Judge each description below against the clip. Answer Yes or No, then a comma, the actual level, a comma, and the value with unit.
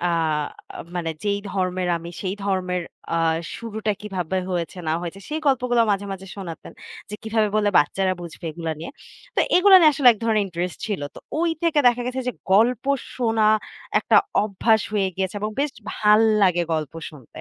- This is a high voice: Yes, high, 200 Hz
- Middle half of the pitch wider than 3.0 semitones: Yes, average, 3.8 semitones